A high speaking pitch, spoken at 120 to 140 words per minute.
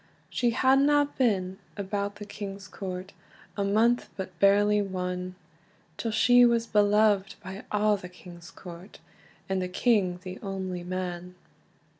Yes: high, 195 Hz; slow, 135 wpm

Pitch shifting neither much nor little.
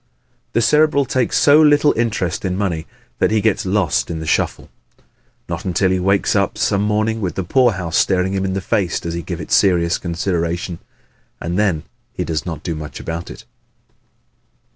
Yes: average, 3.9 semitones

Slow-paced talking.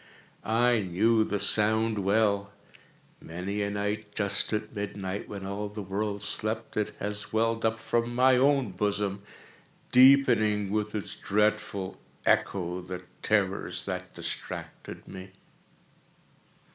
Yes: slow, 120 wpm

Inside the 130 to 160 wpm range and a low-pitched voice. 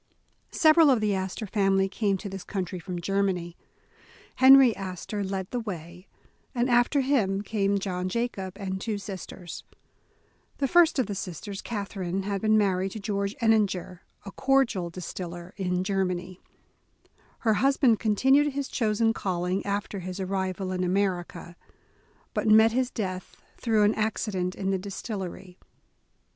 No: average, 155 wpm; high, 195 Hz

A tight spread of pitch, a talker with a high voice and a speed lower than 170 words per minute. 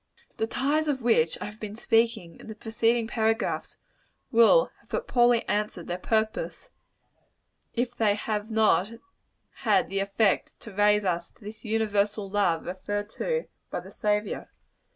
Yes: narrow, 2.1 semitones; high, 220 Hz; average, 150 wpm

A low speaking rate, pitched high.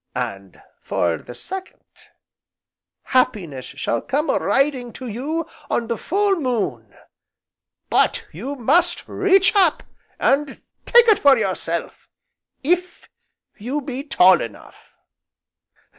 Yes: slow, 115 wpm; very high, 265 Hz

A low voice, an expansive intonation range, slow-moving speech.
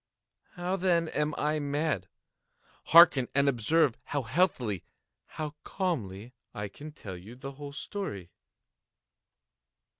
No: medium, 145 Hz; wide, 6.1 semitones; slow, 110 wpm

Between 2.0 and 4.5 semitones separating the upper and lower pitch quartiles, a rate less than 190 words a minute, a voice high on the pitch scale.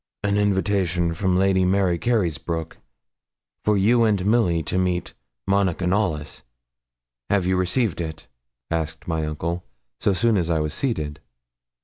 No: average, 3.4 semitones; slow, 135 wpm; very low, 90 Hz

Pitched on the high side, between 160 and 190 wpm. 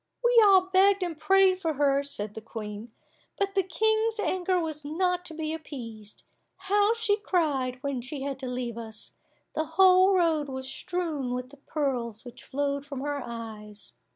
Yes: very high, 295 Hz; average, 175 wpm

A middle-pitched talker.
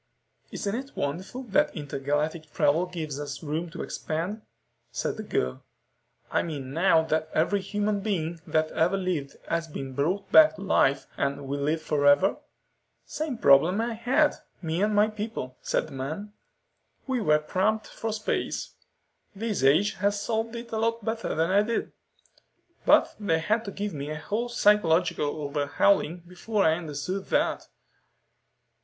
Yes: medium, 175 Hz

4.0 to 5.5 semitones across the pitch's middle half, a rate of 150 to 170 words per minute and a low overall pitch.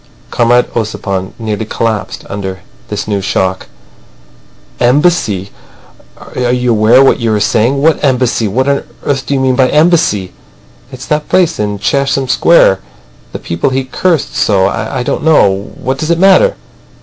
Yes: average, 5.2 semitones; average, 155 wpm; low, 125 Hz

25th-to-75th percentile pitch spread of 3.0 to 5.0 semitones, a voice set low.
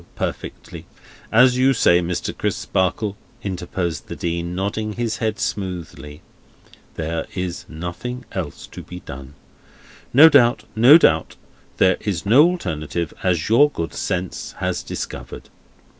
No: wide, 5.4 semitones; very low, 95 Hz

